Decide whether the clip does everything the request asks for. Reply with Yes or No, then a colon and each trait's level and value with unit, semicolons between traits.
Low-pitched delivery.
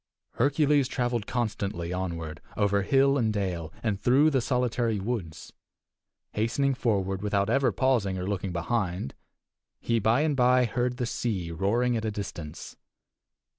Yes: low, 110 Hz